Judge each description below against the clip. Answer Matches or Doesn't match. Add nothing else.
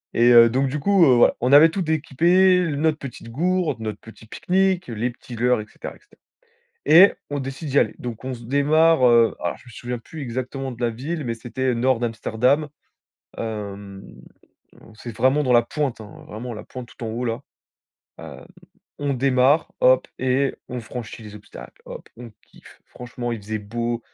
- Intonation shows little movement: Doesn't match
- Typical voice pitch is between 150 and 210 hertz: Doesn't match